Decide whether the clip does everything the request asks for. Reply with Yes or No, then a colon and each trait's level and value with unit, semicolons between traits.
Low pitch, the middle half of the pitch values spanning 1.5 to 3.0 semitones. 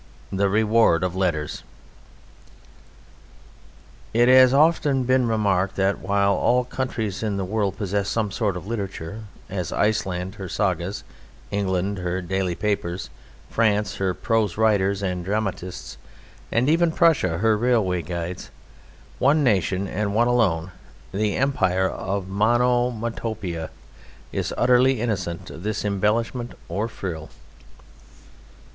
No: low, 100 Hz; average, 3.7 semitones